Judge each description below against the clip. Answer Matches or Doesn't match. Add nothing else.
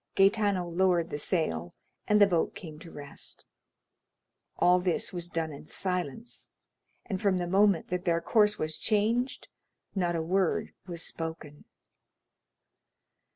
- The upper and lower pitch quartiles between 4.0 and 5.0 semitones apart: Doesn't match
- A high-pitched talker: Doesn't match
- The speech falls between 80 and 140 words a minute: Matches